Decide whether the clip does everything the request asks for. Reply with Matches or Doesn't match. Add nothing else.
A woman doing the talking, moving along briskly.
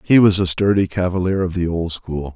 Doesn't match